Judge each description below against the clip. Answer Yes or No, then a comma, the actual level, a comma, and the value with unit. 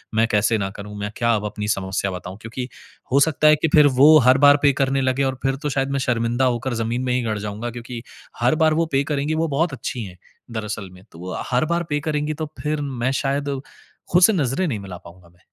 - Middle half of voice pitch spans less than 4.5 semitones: No, average, 5.2 semitones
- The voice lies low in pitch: Yes, low, 125 Hz